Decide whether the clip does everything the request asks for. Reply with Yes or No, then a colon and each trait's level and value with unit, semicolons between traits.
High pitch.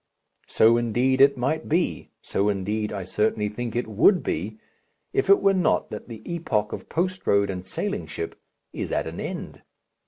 No: low, 115 Hz